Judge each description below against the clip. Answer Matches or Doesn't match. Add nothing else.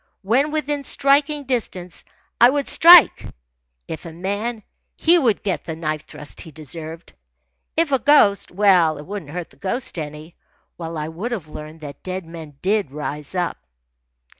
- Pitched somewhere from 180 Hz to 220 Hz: Matches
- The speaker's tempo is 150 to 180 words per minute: Matches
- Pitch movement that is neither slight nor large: Doesn't match